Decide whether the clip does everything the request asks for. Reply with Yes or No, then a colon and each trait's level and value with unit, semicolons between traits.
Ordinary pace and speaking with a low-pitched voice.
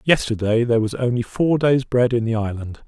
No: fast, 210 wpm; low, 120 Hz